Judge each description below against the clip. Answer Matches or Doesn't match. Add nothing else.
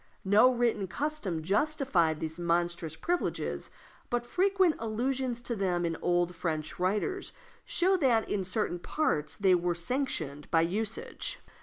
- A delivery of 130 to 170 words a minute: Matches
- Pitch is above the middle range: Matches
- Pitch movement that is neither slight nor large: Doesn't match